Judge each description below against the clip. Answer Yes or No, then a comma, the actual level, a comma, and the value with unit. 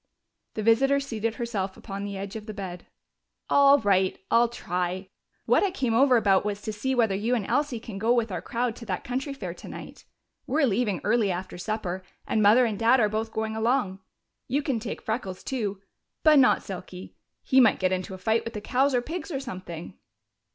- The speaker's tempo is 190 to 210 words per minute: Yes, fast, 205 wpm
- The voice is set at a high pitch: Yes, high, 220 Hz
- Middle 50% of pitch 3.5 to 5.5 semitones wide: Yes, average, 4.2 semitones